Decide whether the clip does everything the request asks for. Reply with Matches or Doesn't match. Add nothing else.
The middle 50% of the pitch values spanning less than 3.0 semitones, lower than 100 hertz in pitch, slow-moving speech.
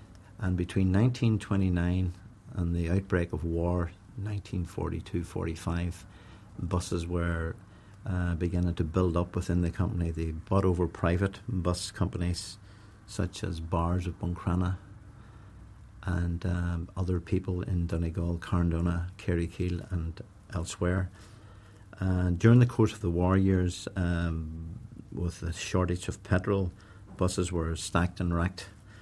Matches